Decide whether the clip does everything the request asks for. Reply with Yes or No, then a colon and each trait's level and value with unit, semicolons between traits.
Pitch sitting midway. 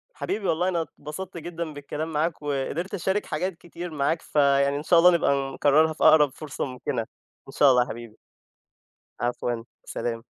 Yes: medium, 150 Hz